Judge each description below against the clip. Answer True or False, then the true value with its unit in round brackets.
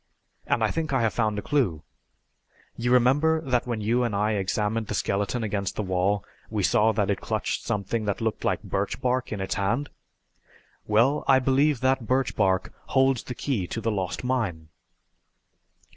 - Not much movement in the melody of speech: False (4.1 semitones)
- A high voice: False (115 Hz)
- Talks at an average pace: True (180 wpm)